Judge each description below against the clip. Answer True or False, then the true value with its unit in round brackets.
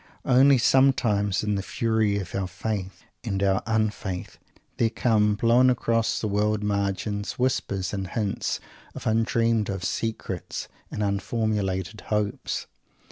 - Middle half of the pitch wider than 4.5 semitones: False (2.4 semitones)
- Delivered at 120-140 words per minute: True (135 wpm)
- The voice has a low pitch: True (105 Hz)